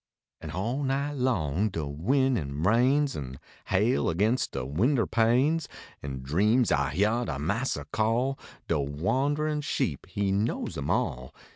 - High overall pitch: No, low, 110 Hz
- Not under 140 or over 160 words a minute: Yes, average, 145 wpm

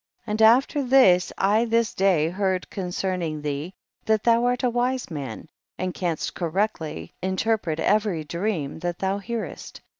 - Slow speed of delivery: No, average, 150 wpm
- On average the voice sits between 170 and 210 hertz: Yes, high, 190 Hz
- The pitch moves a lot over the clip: No, average, 4.7 semitones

